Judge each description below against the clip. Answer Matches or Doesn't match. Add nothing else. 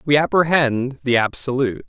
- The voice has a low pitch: Matches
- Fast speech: Doesn't match